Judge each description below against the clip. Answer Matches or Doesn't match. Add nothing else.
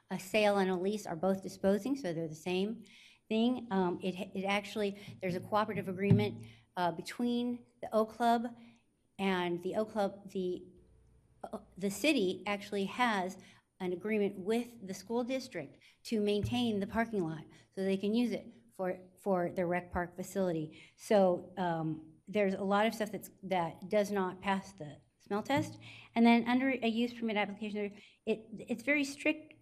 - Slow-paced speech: Doesn't match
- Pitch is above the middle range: Matches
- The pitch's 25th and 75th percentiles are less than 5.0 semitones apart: Matches